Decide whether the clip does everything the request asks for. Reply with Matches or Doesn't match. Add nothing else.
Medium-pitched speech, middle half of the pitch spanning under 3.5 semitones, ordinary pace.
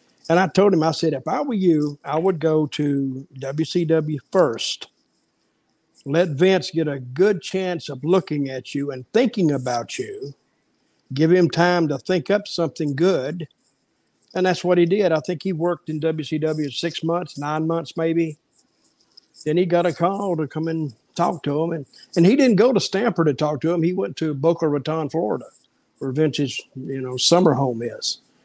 Matches